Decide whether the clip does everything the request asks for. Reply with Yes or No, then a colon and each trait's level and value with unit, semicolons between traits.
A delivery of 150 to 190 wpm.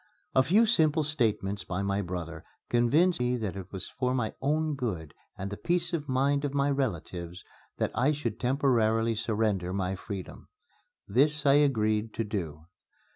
Yes: average, 165 wpm